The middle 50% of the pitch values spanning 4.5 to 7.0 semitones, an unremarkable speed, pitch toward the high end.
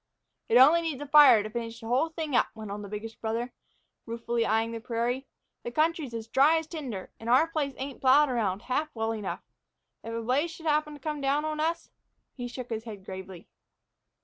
No: average, 4.9 semitones; fast, 210 wpm; high, 245 Hz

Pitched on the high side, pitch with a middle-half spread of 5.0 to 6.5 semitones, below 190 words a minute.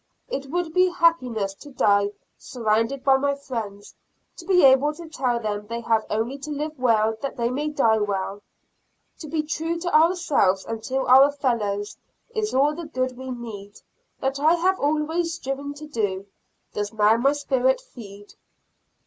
Yes: very high, 265 Hz; wide, 5.5 semitones; average, 170 wpm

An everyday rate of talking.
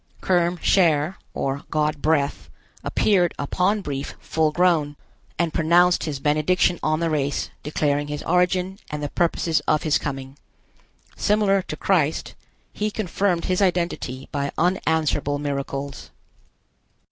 No: slow, 125 wpm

